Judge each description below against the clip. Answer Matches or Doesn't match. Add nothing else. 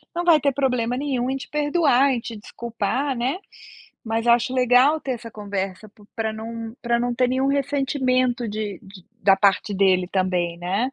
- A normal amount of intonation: Matches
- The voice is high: Matches